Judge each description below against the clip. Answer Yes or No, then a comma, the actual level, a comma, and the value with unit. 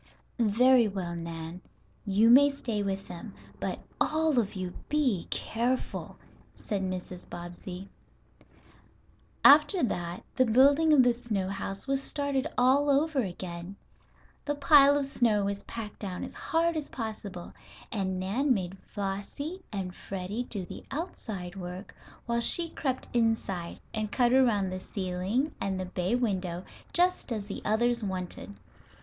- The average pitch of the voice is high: Yes, high, 215 Hz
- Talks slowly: No, average, 145 wpm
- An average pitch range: No, wide, 6.0 semitones